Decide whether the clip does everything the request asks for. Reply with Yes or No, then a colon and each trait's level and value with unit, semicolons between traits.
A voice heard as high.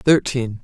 No: low, 125 Hz